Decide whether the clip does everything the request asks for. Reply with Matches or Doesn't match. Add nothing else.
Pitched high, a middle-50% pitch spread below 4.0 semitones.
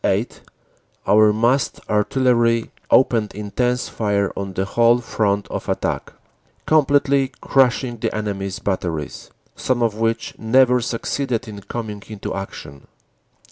Doesn't match